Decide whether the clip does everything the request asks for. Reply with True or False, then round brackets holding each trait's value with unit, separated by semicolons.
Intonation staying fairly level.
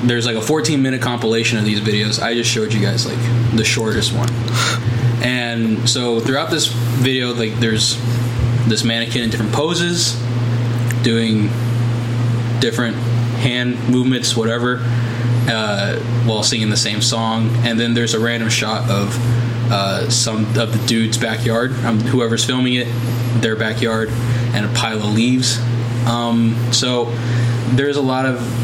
True (0.8 semitones)